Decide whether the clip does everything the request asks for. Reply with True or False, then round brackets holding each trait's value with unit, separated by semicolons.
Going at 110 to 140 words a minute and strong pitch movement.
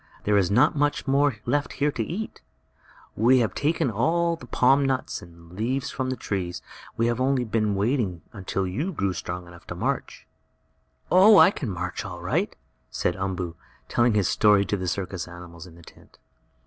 False (185 wpm; 7.0 semitones)